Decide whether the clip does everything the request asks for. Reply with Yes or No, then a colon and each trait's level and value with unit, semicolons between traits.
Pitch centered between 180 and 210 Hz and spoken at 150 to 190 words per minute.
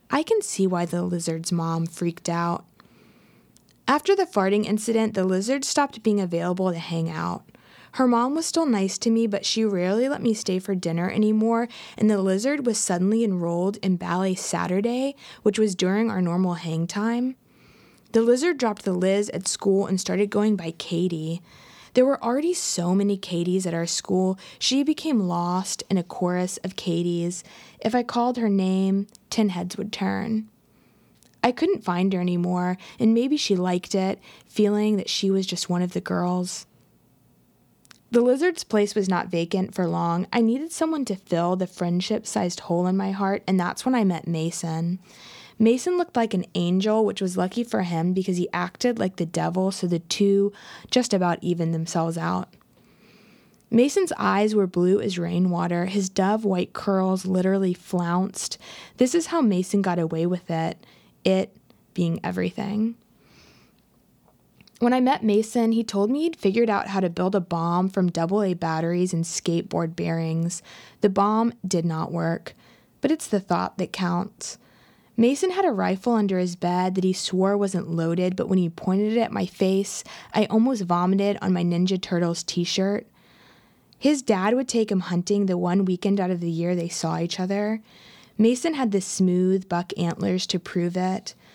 Yes: high, 190 Hz; average, 180 wpm